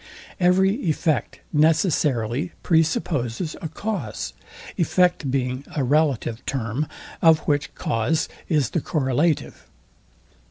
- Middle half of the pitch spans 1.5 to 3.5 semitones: No, average, 4.4 semitones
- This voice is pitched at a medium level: Yes, medium, 150 Hz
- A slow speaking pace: Yes, slow, 105 wpm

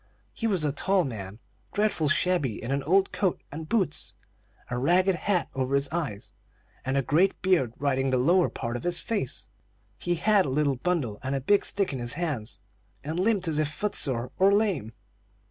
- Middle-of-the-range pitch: Yes, medium, 155 Hz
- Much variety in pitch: Yes, wide, 6.0 semitones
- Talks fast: No, average, 195 wpm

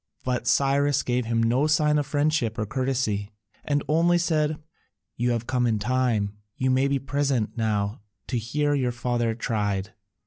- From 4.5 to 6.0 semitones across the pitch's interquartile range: No, average, 4.0 semitones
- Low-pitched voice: Yes, low, 125 Hz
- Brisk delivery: No, average, 165 wpm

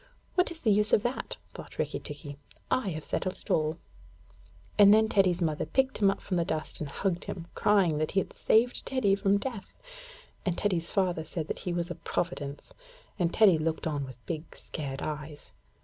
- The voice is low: No, medium, 175 Hz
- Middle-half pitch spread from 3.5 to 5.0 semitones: Yes, average, 4.6 semitones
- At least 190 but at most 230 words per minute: Yes, average, 195 wpm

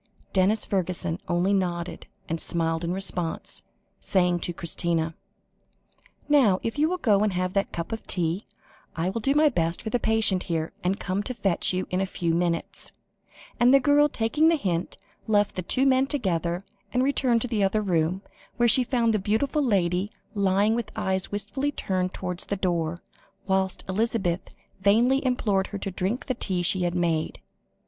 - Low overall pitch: No, high, 195 Hz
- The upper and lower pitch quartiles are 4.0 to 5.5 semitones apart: Yes, average, 4.5 semitones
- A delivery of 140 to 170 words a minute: No, average, 180 wpm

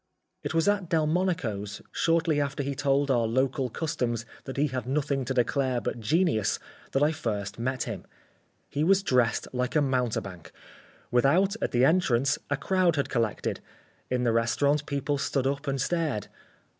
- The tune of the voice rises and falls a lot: No, average, 3.9 semitones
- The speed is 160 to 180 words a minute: Yes, average, 165 wpm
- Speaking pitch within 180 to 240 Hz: No, low, 135 Hz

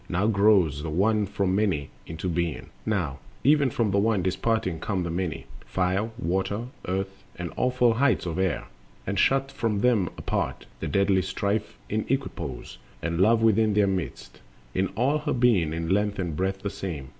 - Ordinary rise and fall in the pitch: Yes, average, 3.6 semitones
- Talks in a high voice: No, low, 100 Hz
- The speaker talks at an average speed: Yes, average, 175 wpm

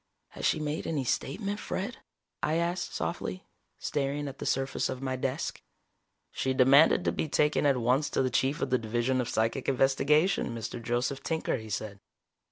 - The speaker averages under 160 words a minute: No, average, 175 wpm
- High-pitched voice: No, low, 135 Hz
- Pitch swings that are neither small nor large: Yes, average, 3.3 semitones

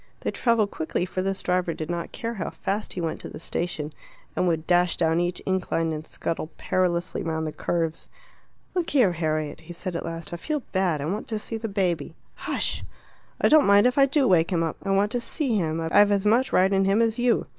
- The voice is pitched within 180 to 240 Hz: Yes, medium, 185 Hz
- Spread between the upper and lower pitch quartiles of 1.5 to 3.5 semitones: No, average, 4.2 semitones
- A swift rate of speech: Yes, fast, 230 wpm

